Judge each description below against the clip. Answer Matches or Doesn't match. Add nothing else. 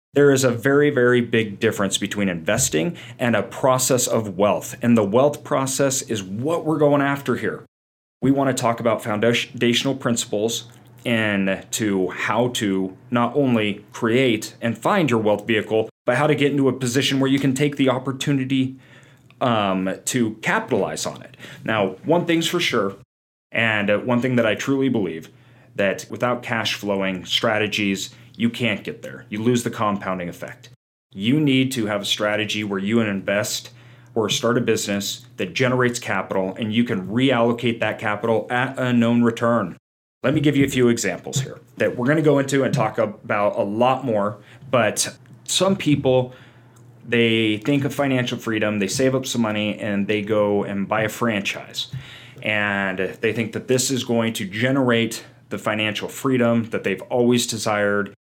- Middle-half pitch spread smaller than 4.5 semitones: Matches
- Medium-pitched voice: Doesn't match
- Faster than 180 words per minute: Doesn't match